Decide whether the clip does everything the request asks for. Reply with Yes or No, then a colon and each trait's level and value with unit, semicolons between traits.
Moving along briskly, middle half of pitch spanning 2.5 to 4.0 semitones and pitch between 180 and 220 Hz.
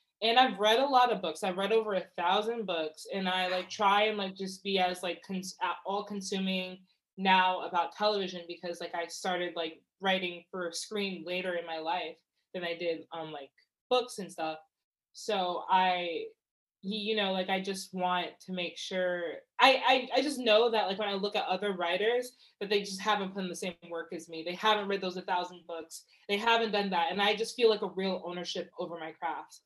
Yes: fast, 215 wpm; average, 3.0 semitones; medium, 185 Hz